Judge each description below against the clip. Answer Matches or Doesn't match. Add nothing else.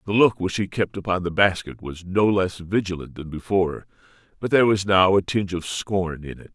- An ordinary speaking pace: Doesn't match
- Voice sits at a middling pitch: Doesn't match